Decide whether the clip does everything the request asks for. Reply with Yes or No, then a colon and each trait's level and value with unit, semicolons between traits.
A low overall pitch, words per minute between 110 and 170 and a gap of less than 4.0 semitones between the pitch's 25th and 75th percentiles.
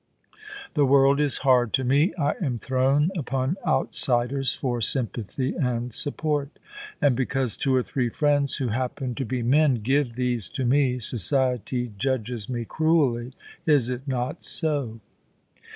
Yes: low, 130 Hz; average, 140 wpm; narrow, 2.5 semitones